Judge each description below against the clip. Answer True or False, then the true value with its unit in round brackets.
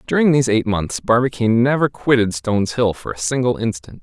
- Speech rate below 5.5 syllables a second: False (5.9 syllables/s)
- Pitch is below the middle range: True (115 Hz)